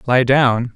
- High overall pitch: No, low, 125 Hz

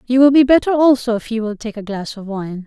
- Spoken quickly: Yes, fast, 290 wpm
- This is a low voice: No, high, 235 Hz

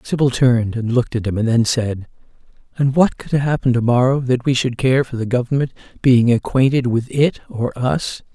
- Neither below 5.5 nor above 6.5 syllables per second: No, 5.2 syllables/s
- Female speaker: No, male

